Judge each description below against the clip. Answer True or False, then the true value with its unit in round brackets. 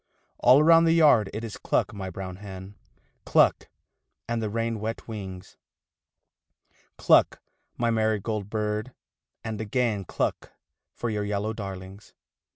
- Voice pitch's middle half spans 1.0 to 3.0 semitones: True (2.5 semitones)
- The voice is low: True (110 Hz)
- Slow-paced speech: True (130 wpm)